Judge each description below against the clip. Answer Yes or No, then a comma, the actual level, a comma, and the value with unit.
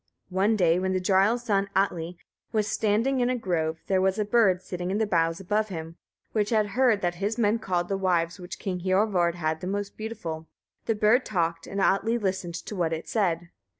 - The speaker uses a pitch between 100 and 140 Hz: No, high, 190 Hz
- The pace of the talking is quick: Yes, fast, 210 wpm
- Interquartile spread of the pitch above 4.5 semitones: No, average, 3.4 semitones